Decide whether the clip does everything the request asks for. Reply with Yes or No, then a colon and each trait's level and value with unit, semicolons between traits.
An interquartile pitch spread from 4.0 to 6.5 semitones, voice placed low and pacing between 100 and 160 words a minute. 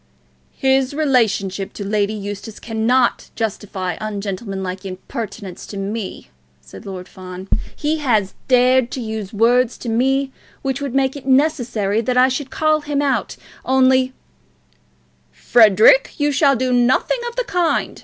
No: average, 4.8 semitones; high, 240 Hz; average, 145 wpm